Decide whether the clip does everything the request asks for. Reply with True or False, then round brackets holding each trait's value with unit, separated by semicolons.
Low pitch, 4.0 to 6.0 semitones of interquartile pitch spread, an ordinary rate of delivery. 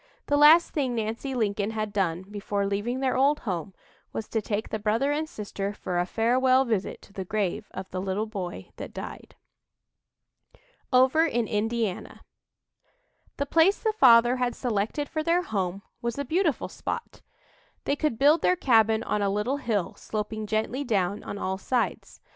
False (225 Hz; 4.8 semitones; 170 wpm)